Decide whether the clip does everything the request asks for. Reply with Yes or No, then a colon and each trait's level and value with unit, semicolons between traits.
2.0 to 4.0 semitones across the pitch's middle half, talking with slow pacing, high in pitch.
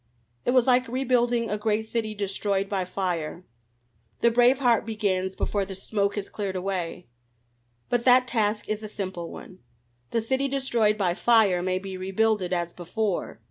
No: average, 3.7 semitones; average, 165 wpm; high, 210 Hz